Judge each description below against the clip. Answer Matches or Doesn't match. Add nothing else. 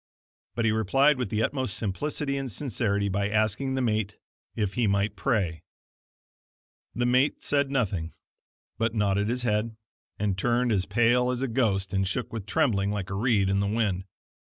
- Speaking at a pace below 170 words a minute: Doesn't match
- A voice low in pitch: Matches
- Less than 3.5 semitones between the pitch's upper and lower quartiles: Doesn't match